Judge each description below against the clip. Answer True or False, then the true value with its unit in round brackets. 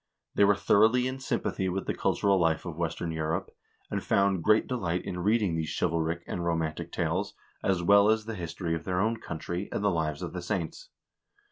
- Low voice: True (90 Hz)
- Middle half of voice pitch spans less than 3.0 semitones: False (3.7 semitones)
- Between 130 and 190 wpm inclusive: False (200 wpm)